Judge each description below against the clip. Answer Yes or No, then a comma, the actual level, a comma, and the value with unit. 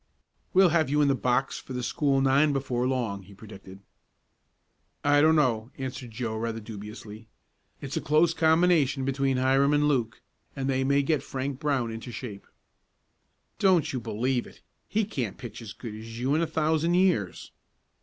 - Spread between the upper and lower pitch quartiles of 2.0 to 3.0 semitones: No, average, 4.5 semitones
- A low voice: Yes, low, 130 Hz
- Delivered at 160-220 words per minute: Yes, average, 175 wpm